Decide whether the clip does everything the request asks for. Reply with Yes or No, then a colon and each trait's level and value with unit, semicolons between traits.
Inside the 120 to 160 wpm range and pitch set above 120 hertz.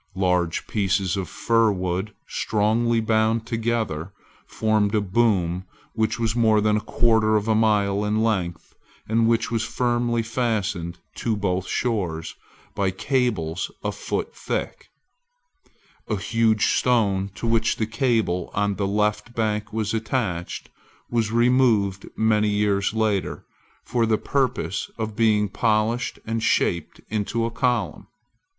No: slow, 135 wpm; low, 110 Hz